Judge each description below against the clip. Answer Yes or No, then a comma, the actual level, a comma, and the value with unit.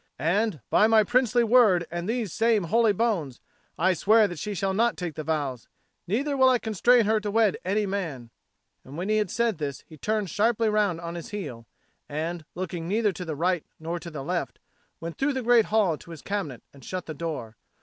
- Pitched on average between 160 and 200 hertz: Yes, high, 190 Hz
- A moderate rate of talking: No, fast, 210 wpm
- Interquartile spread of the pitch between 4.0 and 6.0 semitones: Yes, average, 5.1 semitones